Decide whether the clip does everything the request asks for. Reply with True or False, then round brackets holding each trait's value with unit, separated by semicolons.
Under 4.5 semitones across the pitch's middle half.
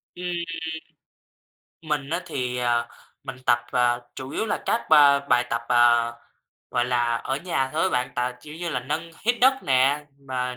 True (3.8 semitones)